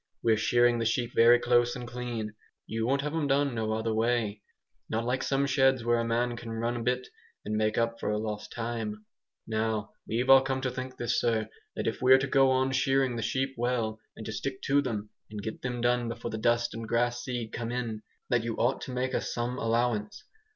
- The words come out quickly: Yes, fast, 220 wpm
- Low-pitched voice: Yes, low, 120 Hz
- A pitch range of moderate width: No, narrow, 2.1 semitones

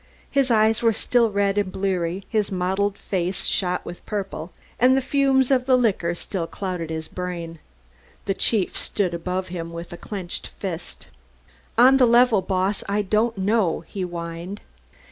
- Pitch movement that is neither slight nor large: Yes, average, 3.9 semitones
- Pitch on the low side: No, high, 195 Hz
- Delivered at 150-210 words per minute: Yes, average, 160 wpm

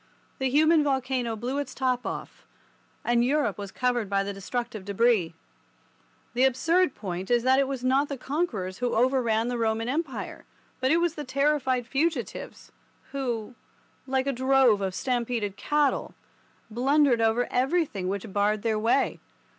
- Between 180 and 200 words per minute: No, average, 155 wpm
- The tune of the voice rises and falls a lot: No, average, 3.6 semitones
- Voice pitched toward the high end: Yes, very high, 250 Hz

